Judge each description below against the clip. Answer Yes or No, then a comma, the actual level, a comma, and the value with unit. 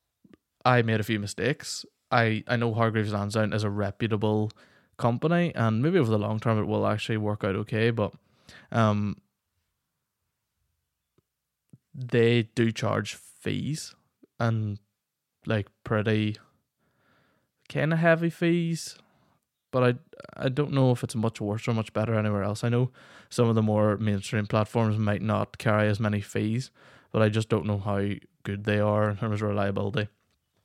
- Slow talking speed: No, average, 155 wpm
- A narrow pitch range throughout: Yes, narrow, 2.3 semitones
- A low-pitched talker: Yes, low, 110 Hz